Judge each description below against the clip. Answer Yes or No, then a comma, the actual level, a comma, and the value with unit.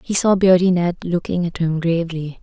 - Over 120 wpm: Yes, average, 200 wpm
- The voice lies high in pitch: No, medium, 175 Hz